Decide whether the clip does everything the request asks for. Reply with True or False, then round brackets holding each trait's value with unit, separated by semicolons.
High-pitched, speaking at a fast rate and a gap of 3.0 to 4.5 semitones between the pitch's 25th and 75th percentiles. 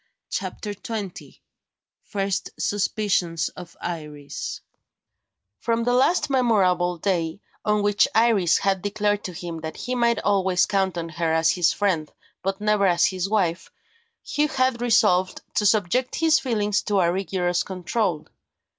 False (195 Hz; 140 wpm; 3.5 semitones)